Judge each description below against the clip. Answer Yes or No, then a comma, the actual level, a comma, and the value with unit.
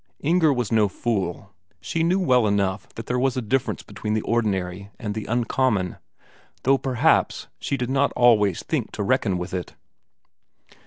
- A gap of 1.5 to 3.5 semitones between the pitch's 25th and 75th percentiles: No, average, 4.7 semitones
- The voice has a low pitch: Yes, low, 115 Hz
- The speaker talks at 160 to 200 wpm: Yes, average, 165 wpm